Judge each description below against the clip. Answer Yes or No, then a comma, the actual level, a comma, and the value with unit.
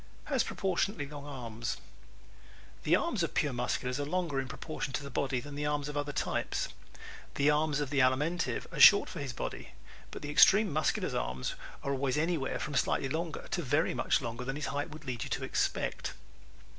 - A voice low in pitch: No, medium, 145 Hz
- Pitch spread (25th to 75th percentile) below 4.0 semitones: Yes, narrow, 2.6 semitones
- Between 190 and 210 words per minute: Yes, average, 200 wpm